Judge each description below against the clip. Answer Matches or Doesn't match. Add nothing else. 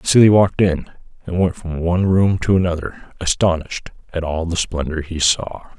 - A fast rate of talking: Doesn't match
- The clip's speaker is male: Matches